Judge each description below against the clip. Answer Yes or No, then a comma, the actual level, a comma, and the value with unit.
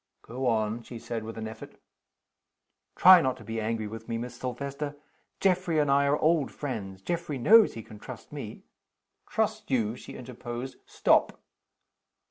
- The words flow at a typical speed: Yes, average, 165 wpm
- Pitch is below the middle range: Yes, low, 125 Hz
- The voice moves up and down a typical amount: Yes, average, 4.8 semitones